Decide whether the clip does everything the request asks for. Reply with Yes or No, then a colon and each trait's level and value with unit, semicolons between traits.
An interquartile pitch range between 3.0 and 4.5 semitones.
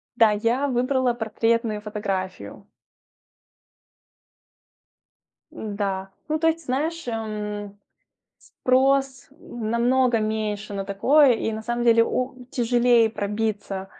Yes: average, 3.4 semitones